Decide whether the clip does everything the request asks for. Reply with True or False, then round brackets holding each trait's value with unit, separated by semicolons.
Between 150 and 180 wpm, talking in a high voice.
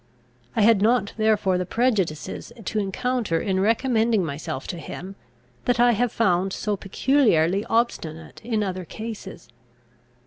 False (135 wpm; 205 Hz)